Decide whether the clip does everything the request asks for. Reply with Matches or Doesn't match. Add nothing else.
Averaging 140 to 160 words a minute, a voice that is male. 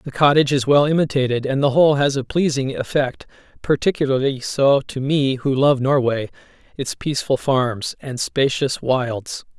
Matches